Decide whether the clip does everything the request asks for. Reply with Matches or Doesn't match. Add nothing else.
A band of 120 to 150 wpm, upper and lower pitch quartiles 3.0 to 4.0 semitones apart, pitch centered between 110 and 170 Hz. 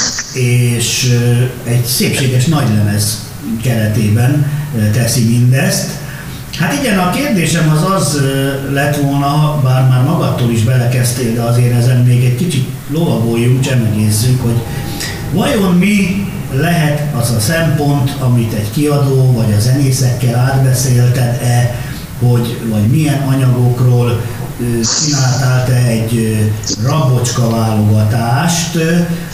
Doesn't match